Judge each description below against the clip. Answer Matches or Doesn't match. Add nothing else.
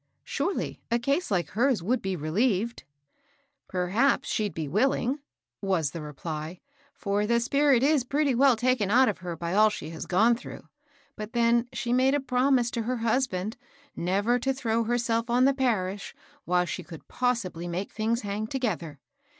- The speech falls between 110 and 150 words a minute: Doesn't match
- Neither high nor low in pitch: Doesn't match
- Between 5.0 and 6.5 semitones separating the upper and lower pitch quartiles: Matches